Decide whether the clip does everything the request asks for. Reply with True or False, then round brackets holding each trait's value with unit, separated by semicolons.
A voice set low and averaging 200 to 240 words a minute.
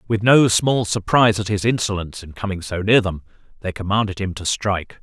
True (100 Hz; 205 wpm)